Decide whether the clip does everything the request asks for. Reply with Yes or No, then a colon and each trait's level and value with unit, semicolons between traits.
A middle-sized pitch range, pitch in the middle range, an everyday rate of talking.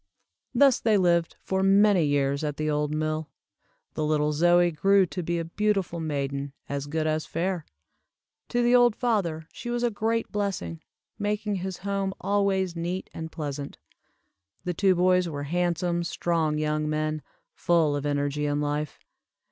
Yes: average, 4.3 semitones; medium, 170 Hz; average, 160 wpm